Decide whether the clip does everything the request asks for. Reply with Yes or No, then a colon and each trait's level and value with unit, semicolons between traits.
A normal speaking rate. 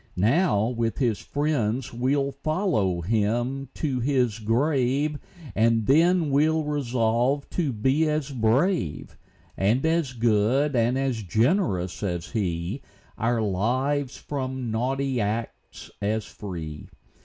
No: slow, 115 wpm